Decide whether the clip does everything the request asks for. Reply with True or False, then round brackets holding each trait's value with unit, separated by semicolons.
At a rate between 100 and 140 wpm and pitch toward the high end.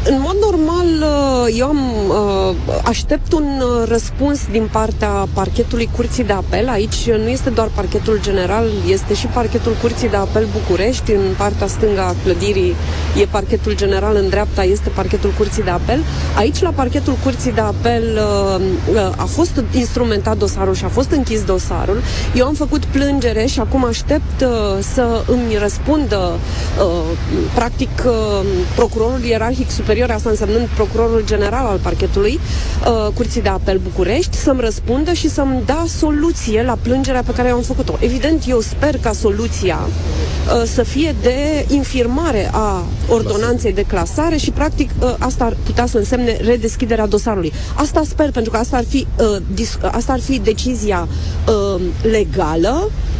False (155 wpm; 235 Hz)